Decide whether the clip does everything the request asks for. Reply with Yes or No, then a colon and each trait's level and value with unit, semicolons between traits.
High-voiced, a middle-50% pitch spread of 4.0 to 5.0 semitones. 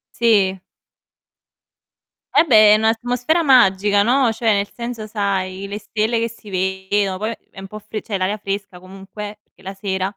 No: high, 205 Hz; narrow, 2.6 semitones